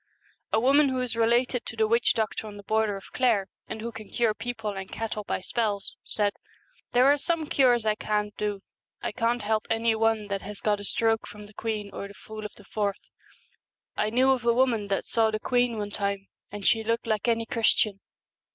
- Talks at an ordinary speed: No, fast, 225 wpm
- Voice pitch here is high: Yes, high, 220 Hz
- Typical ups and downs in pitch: No, narrow, 2.2 semitones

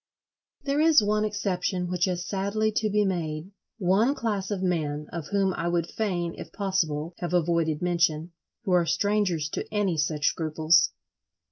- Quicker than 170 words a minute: No, average, 155 wpm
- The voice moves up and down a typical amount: Yes, average, 3.6 semitones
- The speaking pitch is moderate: Yes, medium, 180 Hz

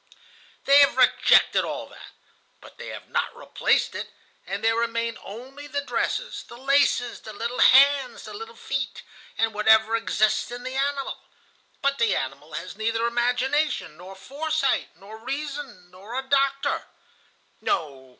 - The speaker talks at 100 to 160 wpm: Yes, average, 150 wpm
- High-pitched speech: Yes, high, 240 Hz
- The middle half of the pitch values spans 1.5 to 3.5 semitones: No, average, 4.2 semitones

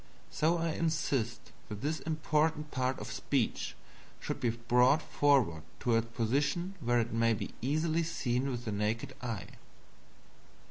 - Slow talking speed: No, average, 145 wpm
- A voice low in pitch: Yes, low, 130 Hz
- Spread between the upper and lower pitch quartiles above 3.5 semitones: Yes, average, 5.0 semitones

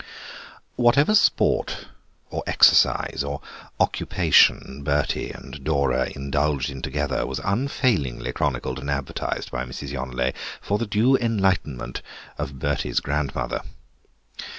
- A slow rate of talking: Yes, slow, 110 wpm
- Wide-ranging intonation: Yes, wide, 7.3 semitones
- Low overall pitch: Yes, very low, 70 Hz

